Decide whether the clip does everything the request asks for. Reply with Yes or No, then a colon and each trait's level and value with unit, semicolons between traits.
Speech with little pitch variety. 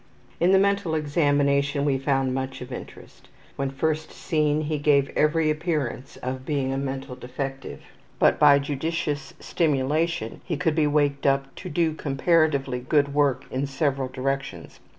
Yes: narrow, 2.3 semitones